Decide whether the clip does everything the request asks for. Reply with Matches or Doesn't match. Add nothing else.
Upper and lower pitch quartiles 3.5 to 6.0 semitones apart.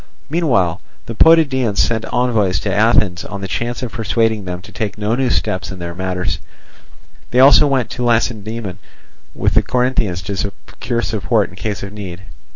Matches